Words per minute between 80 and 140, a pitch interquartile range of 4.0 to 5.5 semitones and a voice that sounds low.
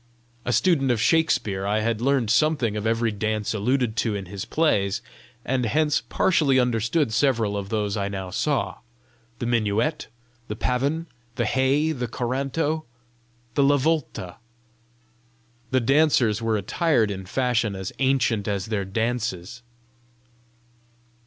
Yes: slow, 135 wpm; average, 4.5 semitones; low, 115 Hz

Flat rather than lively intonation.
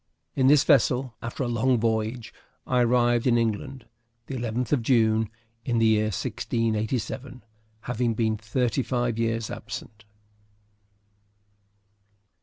Yes: narrow, 2.1 semitones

